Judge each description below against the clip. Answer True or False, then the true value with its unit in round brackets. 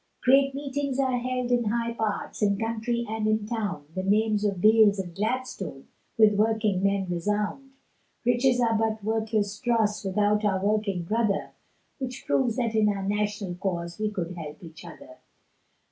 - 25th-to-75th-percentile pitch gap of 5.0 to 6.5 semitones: False (2.9 semitones)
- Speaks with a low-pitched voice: False (215 Hz)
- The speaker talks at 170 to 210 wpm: False (160 wpm)